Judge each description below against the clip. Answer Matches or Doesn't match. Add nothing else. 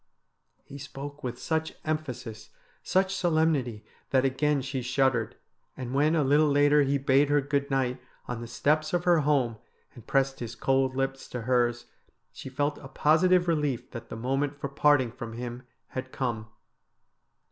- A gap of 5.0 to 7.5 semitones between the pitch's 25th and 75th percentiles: Doesn't match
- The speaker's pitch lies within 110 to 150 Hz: Matches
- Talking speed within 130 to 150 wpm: Doesn't match